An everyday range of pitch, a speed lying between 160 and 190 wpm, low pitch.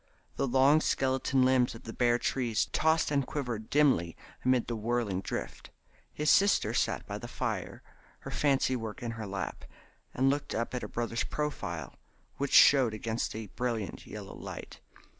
Yes: average, 3.4 semitones; average, 165 wpm; low, 125 Hz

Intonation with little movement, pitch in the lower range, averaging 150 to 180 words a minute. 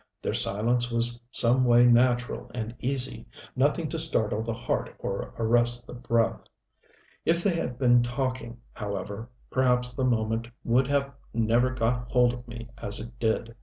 Yes: narrow, 1.6 semitones; low, 120 Hz; average, 160 wpm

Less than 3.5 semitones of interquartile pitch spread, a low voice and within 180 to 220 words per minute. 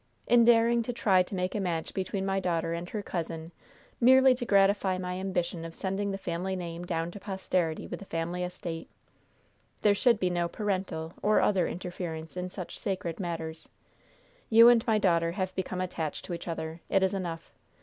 No: average, 2.9 semitones; medium, 185 Hz; average, 190 wpm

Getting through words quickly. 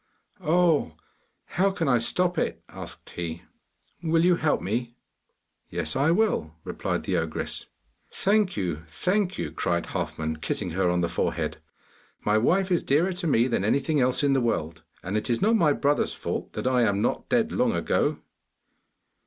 No: average, 170 wpm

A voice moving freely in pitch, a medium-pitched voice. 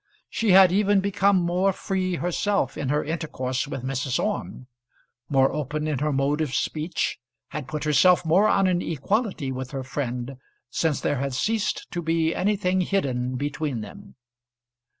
Yes: wide, 5.7 semitones; medium, 155 Hz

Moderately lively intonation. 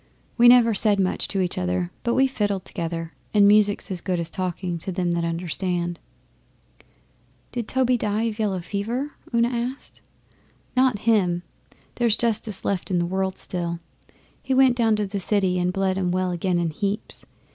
Yes: average, 4.2 semitones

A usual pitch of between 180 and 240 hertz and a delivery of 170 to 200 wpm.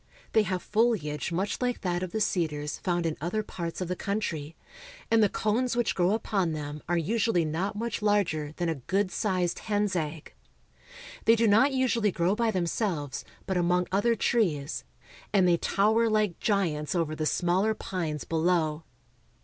Yes: medium, 185 Hz; average, 175 wpm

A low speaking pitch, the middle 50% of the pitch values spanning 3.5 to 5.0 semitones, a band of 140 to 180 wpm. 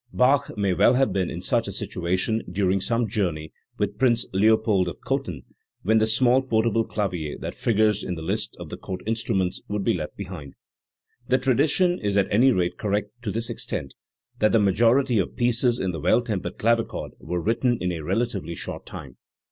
No: low, 105 Hz; average, 4.3 semitones; average, 190 wpm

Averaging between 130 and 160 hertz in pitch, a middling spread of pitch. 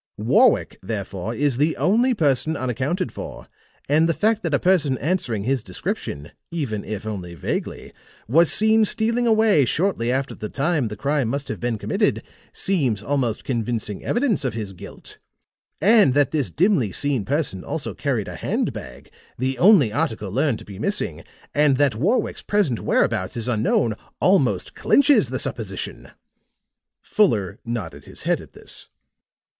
No: low, 135 Hz; wide, 7.7 semitones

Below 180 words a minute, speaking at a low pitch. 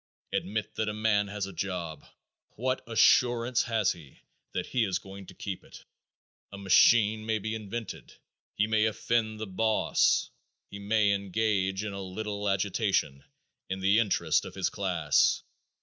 Yes: average, 155 wpm; low, 105 Hz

